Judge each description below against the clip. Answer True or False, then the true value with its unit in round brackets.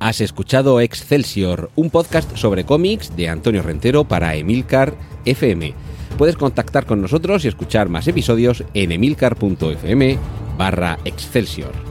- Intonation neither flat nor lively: False (7.4 semitones)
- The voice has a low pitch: True (115 Hz)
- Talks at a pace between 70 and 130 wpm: True (125 wpm)